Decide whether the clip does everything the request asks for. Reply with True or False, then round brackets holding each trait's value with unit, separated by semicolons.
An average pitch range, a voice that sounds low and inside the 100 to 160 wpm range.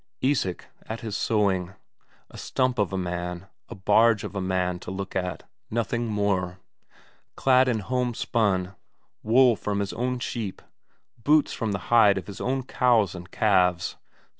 True (4.2 semitones; 105 Hz; 155 wpm)